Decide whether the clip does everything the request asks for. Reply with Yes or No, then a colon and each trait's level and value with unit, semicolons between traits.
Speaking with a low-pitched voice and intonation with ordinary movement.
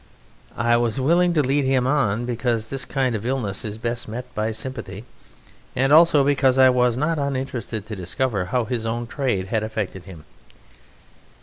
Yes: low, 120 Hz; average, 3.5 semitones